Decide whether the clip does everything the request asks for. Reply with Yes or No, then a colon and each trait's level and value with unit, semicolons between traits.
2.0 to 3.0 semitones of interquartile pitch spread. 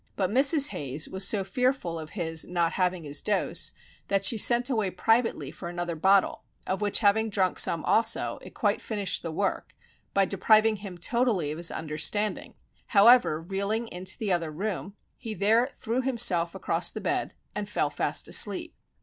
No: average, 4.3 semitones